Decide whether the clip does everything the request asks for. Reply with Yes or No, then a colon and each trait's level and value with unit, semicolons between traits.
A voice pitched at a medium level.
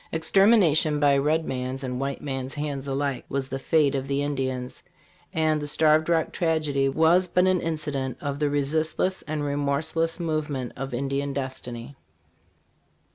Yes: medium, 145 Hz